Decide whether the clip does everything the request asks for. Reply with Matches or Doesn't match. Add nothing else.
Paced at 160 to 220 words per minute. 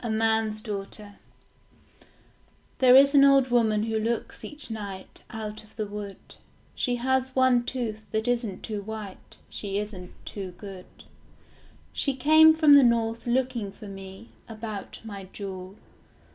Doesn't match